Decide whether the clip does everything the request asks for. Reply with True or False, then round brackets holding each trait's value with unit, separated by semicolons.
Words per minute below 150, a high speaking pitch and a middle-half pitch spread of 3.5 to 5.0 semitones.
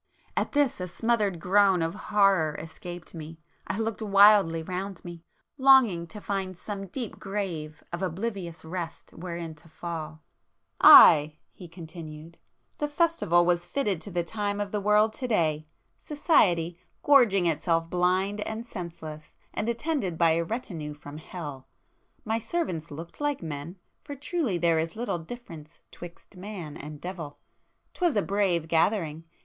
False (140 wpm; 180 Hz; 4.2 semitones)